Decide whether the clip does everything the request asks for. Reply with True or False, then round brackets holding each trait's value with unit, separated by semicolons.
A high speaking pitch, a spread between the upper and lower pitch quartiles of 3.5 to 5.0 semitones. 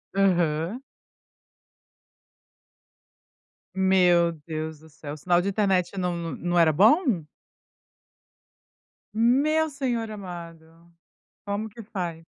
False (180 Hz; 4.2 semitones)